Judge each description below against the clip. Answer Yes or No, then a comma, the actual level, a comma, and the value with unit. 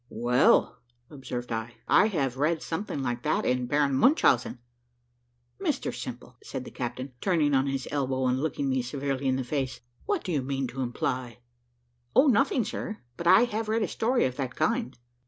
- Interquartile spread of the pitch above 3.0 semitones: Yes, average, 5.1 semitones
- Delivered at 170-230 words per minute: Yes, average, 180 wpm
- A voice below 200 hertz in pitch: Yes, low, 135 Hz